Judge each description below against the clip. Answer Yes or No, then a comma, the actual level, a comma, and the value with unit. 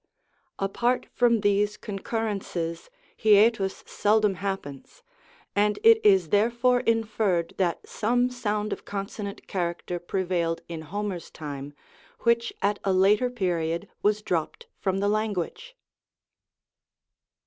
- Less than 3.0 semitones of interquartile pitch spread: No, average, 3.7 semitones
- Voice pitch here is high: Yes, high, 205 Hz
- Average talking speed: No, slow, 115 wpm